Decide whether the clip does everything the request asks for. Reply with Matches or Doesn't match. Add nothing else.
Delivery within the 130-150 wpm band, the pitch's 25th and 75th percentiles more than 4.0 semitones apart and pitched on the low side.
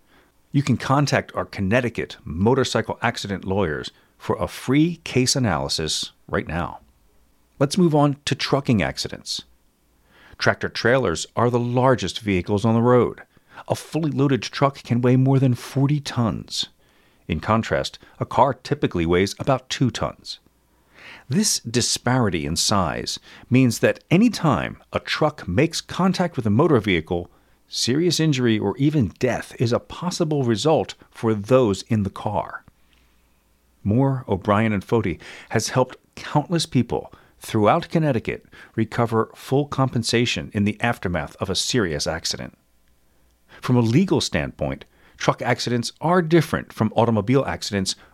Matches